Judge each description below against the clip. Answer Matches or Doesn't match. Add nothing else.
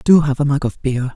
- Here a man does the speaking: Matches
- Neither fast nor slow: Doesn't match